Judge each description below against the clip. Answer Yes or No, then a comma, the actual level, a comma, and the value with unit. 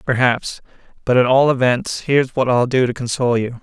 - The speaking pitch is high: No, low, 125 Hz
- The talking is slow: No, average, 200 wpm